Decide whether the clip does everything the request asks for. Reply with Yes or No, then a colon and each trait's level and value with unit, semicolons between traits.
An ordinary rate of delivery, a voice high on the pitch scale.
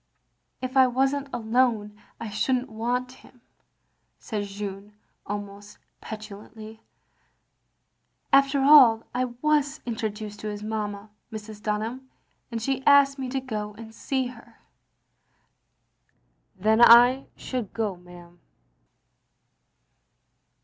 No: slow, 120 wpm; high, 225 Hz